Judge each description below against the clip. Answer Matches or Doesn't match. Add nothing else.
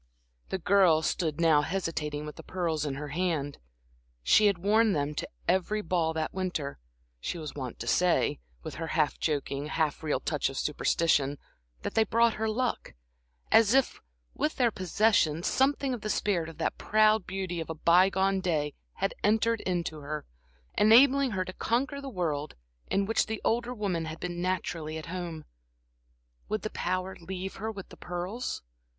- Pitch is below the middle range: Doesn't match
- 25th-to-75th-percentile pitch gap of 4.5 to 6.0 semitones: Matches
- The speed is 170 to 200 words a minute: Matches